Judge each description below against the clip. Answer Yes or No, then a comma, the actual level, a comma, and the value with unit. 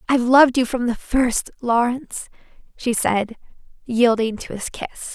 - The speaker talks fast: No, average, 150 wpm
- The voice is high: Yes, high, 240 Hz